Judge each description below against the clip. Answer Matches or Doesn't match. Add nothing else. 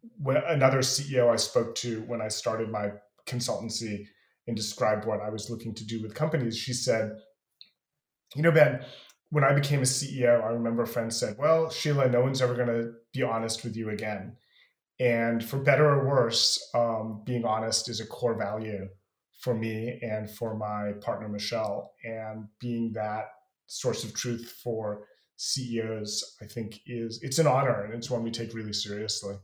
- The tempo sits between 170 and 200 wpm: Matches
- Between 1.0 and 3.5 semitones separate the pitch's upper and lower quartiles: Matches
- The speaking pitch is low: Matches